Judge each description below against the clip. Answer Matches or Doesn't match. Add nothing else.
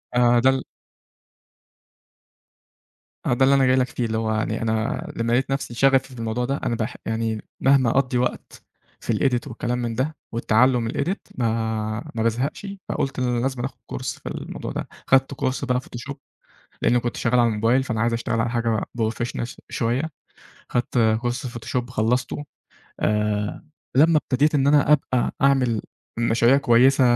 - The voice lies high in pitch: Doesn't match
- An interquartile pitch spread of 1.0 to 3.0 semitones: Matches